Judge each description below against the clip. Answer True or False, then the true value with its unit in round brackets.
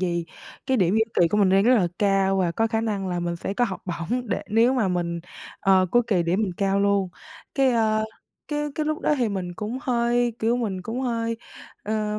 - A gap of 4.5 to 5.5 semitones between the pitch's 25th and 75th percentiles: False (4.0 semitones)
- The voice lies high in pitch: True (210 Hz)